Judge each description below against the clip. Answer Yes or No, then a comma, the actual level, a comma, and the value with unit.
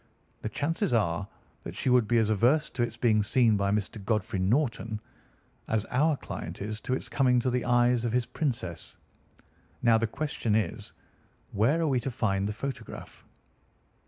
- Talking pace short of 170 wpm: No, average, 175 wpm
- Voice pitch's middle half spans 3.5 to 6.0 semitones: No, average, 3.1 semitones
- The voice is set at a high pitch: No, low, 115 Hz